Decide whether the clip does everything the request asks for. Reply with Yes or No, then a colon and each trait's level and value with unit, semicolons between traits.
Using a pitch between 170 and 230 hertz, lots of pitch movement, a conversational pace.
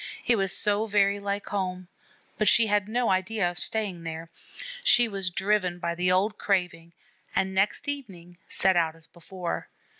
No: high, 190 Hz; average, 2.8 semitones; average, 170 wpm